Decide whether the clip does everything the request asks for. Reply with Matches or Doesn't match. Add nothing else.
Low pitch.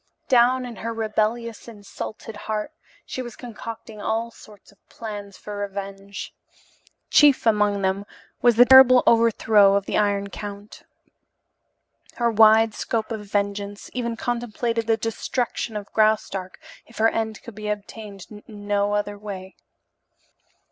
Doesn't match